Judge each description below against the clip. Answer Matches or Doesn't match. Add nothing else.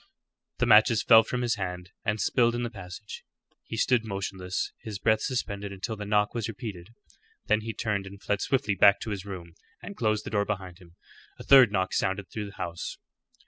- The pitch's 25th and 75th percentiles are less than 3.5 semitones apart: Matches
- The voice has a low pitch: Matches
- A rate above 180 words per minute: Matches